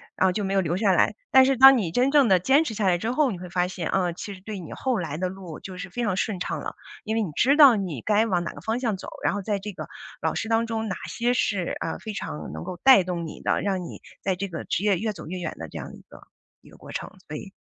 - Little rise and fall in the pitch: No, average, 3.9 semitones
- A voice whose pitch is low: No, high, 195 Hz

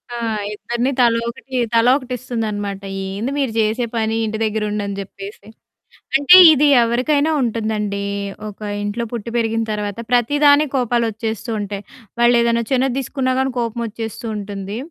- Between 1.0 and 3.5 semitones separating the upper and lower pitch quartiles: Yes, average, 2.9 semitones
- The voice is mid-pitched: No, high, 230 Hz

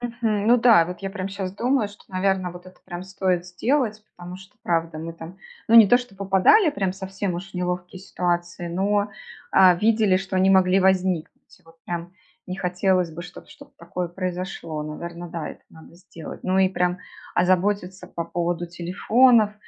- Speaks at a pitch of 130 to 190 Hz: Yes, medium, 185 Hz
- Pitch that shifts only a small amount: Yes, narrow, 2.2 semitones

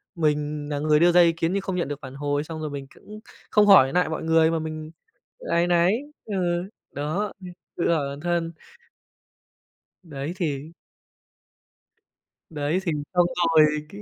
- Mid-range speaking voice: Yes, medium, 160 Hz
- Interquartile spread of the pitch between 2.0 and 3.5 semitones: Yes, average, 3.0 semitones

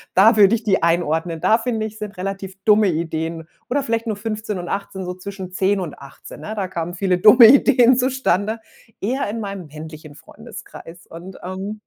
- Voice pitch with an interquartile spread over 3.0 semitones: Yes, average, 4.0 semitones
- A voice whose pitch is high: Yes, high, 195 Hz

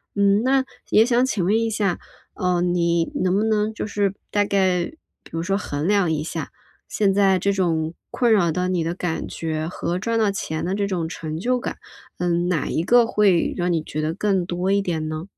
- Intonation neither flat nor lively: Yes, average, 3.4 semitones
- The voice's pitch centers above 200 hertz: No, medium, 185 Hz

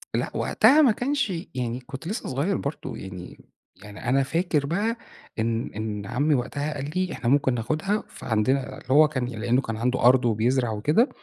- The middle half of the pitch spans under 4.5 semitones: No, average, 5.1 semitones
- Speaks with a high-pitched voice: No, low, 135 Hz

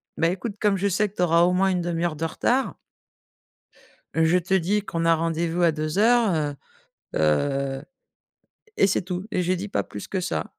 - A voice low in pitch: No, medium, 175 Hz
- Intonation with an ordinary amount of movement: Yes, average, 3.0 semitones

